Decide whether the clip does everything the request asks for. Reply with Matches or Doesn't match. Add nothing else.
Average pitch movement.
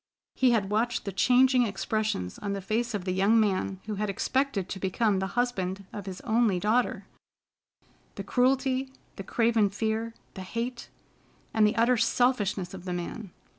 Matches